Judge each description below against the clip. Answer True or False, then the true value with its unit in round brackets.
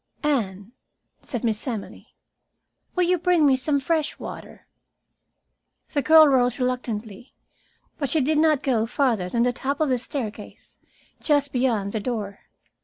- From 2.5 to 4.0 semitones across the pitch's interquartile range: False (4.7 semitones)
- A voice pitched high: True (255 Hz)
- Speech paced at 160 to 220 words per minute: False (145 wpm)